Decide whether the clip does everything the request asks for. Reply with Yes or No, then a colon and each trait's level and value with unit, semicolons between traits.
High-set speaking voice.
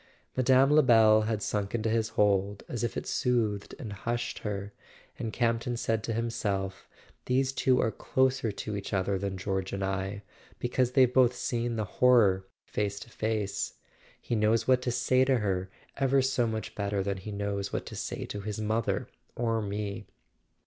No: low, 110 Hz